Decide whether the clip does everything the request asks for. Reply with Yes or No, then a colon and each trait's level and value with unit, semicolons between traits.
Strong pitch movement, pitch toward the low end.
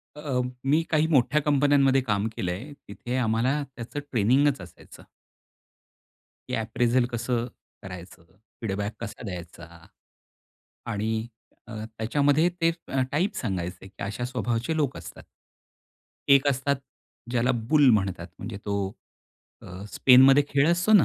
Yes: wide, 5.7 semitones; low, 120 Hz